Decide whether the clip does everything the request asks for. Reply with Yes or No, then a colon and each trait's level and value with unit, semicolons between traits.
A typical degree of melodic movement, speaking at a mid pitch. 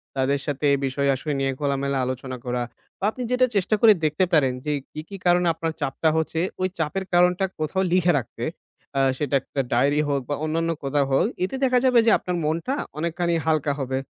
Yes: average, 4.4 semitones; medium, 155 Hz